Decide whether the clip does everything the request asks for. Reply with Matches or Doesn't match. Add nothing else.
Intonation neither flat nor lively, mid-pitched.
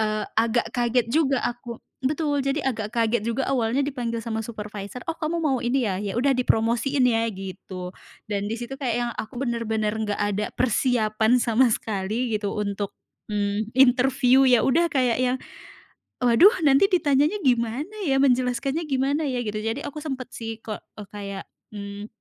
Doesn't match